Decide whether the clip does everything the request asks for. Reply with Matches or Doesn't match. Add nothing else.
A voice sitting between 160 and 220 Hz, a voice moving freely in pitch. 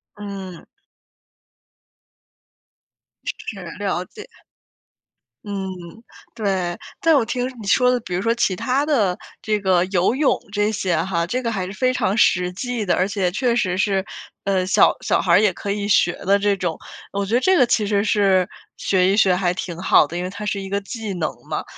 Doesn't match